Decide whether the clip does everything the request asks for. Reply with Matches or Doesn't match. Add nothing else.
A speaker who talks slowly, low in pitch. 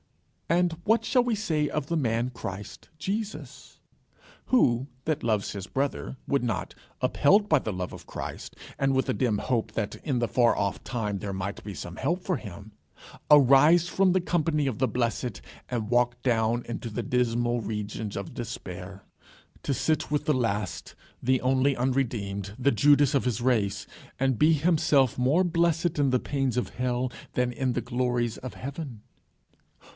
Doesn't match